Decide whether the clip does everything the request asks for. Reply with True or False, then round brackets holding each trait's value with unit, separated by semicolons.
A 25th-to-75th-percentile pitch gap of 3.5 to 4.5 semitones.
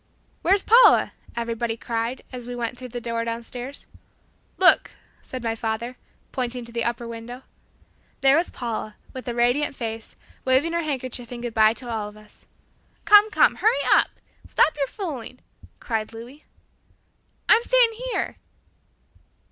False (3.0 semitones)